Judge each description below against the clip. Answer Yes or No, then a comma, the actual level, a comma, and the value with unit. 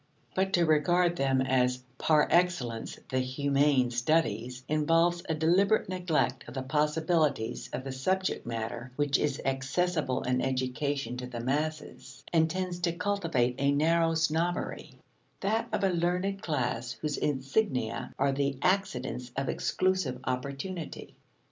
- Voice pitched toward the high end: No, medium, 145 Hz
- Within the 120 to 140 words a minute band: Yes, slow, 135 wpm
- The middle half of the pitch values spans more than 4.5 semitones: Yes, average, 5.0 semitones